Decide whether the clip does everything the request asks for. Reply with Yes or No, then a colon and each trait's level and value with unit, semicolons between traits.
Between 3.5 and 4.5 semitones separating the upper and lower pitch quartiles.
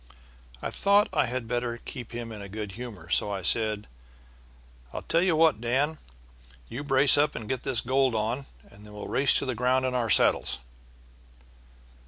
Yes: average, 3.8 semitones